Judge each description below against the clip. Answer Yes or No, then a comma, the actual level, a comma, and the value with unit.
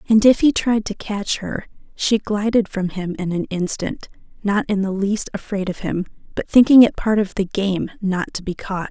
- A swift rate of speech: Yes, fast, 215 wpm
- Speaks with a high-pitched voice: Yes, high, 200 Hz